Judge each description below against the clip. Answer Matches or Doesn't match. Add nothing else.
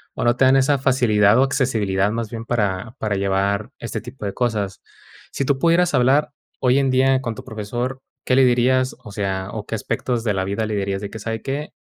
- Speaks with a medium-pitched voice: Doesn't match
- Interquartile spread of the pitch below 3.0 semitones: Doesn't match